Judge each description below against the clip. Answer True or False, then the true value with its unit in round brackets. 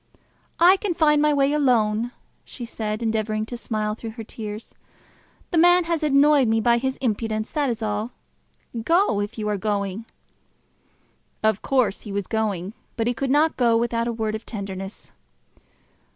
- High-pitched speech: True (230 Hz)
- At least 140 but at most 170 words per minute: True (165 wpm)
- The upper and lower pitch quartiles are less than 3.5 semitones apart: False (4.3 semitones)